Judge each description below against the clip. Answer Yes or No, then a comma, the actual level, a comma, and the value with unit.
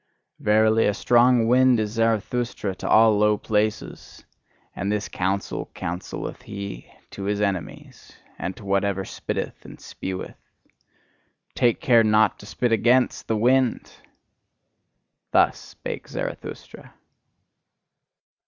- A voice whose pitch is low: Yes, low, 110 Hz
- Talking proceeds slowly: Yes, slow, 115 wpm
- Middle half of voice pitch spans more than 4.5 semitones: No, average, 2.8 semitones